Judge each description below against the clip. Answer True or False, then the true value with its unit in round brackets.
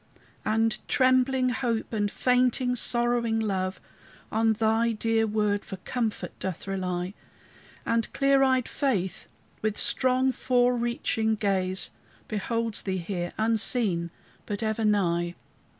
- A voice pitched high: True (220 Hz)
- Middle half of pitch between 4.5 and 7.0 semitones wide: False (3.6 semitones)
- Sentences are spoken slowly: True (115 wpm)